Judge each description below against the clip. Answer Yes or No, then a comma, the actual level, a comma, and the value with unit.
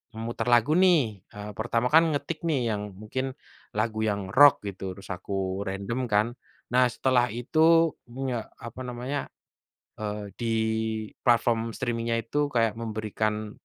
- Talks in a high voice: No, low, 115 Hz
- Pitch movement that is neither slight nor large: Yes, average, 3.3 semitones